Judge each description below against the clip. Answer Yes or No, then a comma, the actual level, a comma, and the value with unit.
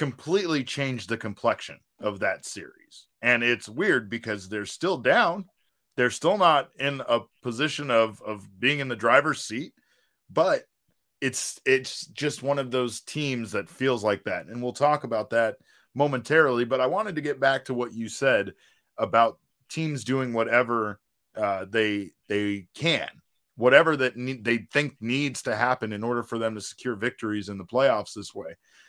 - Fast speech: No, average, 170 wpm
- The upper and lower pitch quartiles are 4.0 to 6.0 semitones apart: No, average, 3.4 semitones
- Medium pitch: No, low, 120 Hz